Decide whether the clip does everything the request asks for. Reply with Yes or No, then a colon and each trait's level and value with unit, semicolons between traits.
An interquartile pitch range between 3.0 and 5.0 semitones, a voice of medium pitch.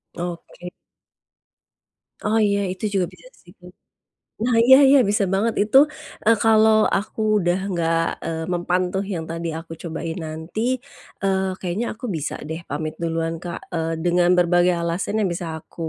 Yes: average, 3.4 semitones; medium, 175 Hz